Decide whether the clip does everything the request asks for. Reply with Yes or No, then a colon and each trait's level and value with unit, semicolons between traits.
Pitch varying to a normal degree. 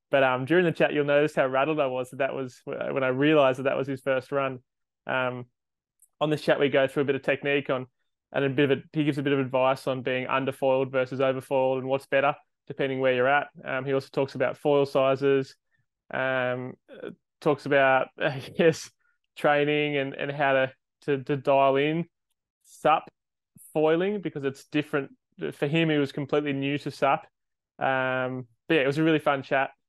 No: narrow, 1.9 semitones